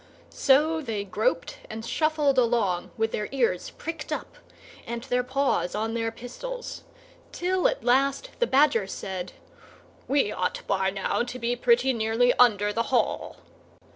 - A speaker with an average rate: Yes, average, 145 wpm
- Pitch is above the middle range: Yes, high, 245 Hz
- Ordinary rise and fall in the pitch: Yes, average, 3.9 semitones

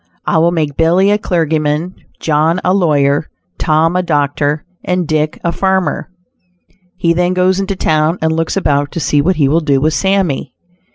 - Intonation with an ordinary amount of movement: Yes, average, 3.4 semitones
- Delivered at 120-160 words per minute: No, average, 175 wpm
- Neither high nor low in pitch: Yes, medium, 160 Hz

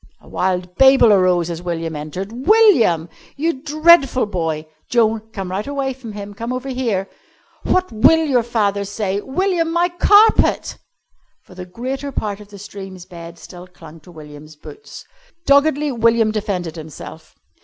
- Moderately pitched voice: No, high, 210 Hz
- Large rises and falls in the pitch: Yes, wide, 7.0 semitones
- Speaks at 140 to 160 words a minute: Yes, average, 155 wpm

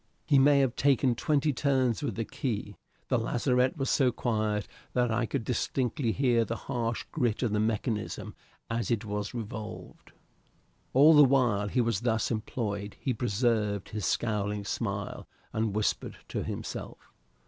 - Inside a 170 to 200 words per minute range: No, average, 155 wpm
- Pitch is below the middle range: Yes, low, 115 Hz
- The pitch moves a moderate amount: Yes, average, 3.3 semitones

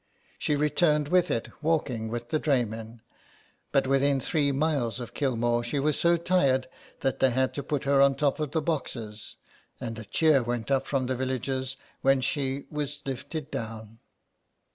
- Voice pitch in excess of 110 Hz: Yes, low, 135 Hz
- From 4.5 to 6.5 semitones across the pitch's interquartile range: No, average, 3.5 semitones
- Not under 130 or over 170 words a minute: No, average, 180 wpm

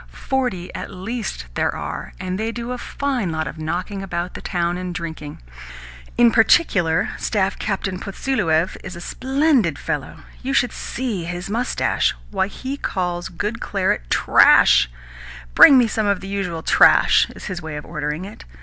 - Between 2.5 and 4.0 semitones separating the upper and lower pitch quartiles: No, average, 5.0 semitones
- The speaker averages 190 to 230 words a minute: No, average, 170 wpm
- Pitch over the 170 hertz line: Yes, high, 190 Hz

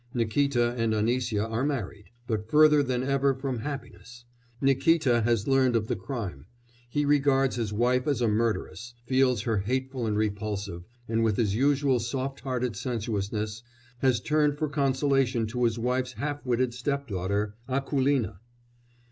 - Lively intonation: No, average, 3.6 semitones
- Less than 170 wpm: Yes, average, 150 wpm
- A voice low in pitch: Yes, low, 125 Hz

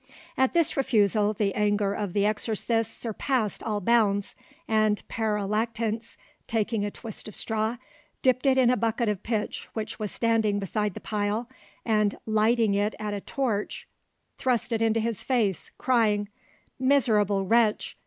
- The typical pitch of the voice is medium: No, high, 220 Hz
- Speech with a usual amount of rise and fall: No, narrow, 2.0 semitones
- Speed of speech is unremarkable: Yes, average, 155 wpm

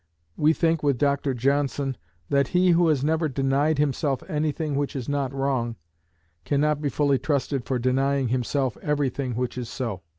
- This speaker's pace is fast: No, average, 165 wpm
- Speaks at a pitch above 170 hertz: No, medium, 140 Hz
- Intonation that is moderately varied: No, narrow, 2.3 semitones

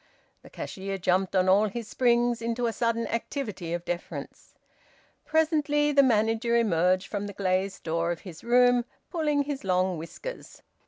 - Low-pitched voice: No, high, 225 Hz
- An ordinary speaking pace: Yes, average, 155 wpm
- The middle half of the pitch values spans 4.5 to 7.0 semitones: Yes, average, 5.0 semitones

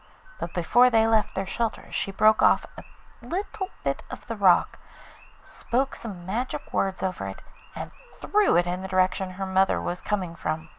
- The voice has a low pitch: No, high, 190 Hz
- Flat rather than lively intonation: No, average, 4.0 semitones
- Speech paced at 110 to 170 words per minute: No, average, 180 wpm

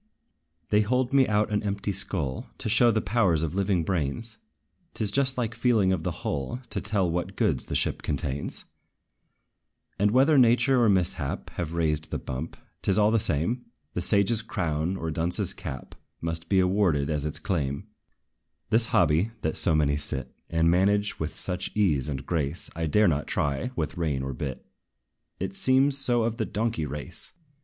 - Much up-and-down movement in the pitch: Yes, wide, 5.9 semitones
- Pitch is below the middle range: Yes, very low, 90 Hz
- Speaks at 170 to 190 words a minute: Yes, average, 180 wpm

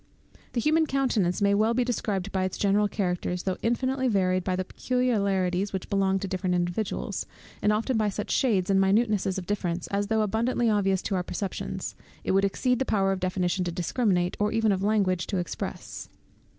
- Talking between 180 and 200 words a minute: Yes, average, 190 wpm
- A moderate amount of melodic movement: Yes, average, 3.0 semitones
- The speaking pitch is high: Yes, high, 200 Hz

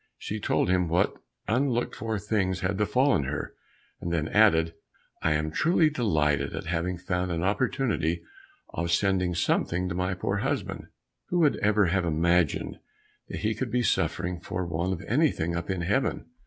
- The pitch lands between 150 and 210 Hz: No, very low, 90 Hz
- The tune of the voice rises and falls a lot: No, average, 4.2 semitones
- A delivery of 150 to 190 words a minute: Yes, average, 170 wpm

